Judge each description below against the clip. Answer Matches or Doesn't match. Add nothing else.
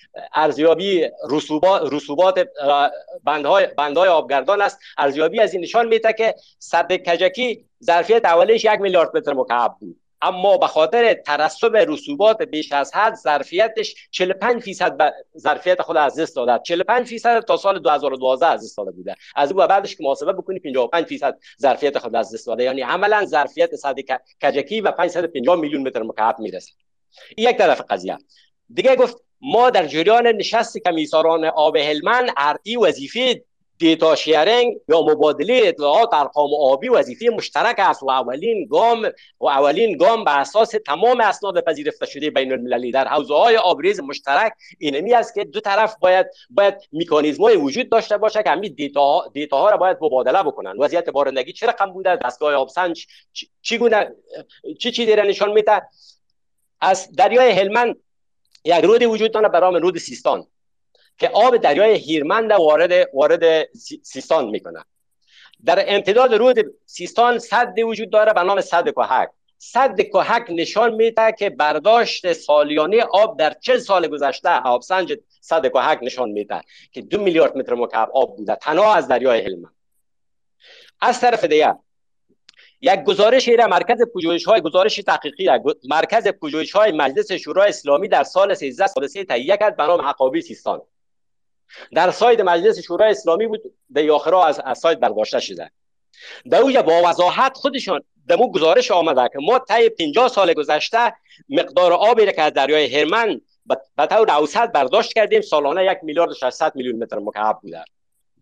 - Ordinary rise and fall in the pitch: Doesn't match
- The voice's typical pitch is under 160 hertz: Doesn't match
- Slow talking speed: Doesn't match